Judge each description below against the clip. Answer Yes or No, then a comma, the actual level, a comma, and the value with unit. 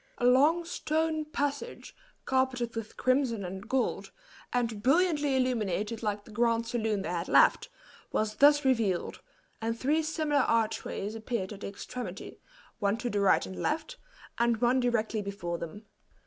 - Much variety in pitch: No, average, 4.5 semitones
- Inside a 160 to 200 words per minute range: No, average, 150 wpm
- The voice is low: No, high, 235 Hz